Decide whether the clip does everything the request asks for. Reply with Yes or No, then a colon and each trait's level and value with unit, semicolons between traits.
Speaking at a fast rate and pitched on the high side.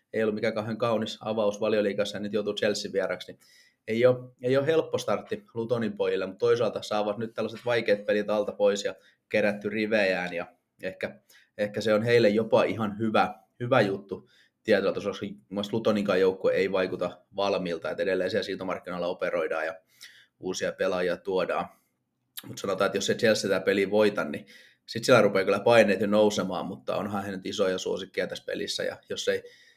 No: fast, 180 wpm; low, 120 Hz